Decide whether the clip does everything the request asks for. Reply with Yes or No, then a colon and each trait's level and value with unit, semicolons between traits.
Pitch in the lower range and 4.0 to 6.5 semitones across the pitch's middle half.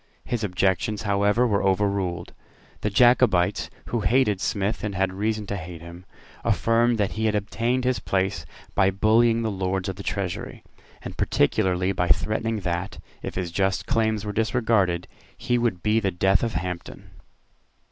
No: low, 100 Hz; average, 3.0 semitones